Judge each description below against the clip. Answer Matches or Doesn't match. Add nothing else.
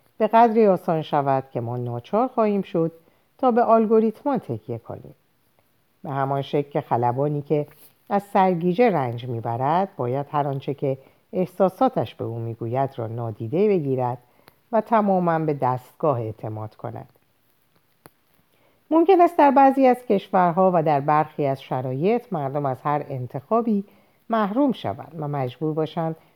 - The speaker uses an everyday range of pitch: Doesn't match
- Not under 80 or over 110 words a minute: Doesn't match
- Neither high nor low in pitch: Matches